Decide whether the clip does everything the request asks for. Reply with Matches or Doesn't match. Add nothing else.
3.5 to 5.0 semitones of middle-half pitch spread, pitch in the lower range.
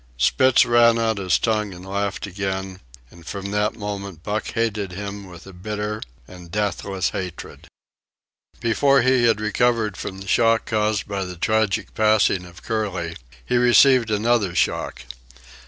Doesn't match